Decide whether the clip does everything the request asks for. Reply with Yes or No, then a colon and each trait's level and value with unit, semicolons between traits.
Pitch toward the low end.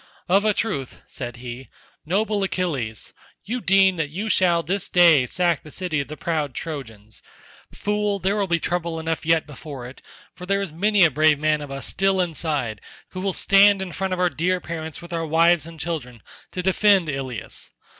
No: medium, 170 Hz